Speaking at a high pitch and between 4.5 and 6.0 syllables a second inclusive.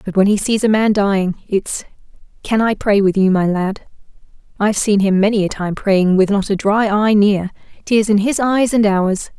Yes: high, 205 Hz; 4.9 syllables/s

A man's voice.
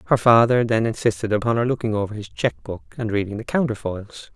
Yes: male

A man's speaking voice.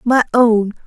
No: female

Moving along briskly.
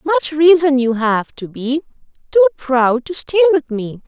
No: average, 175 wpm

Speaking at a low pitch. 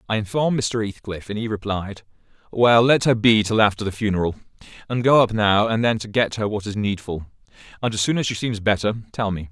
Yes: low, 110 Hz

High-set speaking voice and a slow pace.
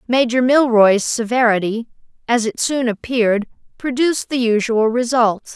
Yes: high, 235 Hz; slow, 120 wpm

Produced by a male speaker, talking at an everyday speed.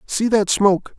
Yes: male; average, 185 wpm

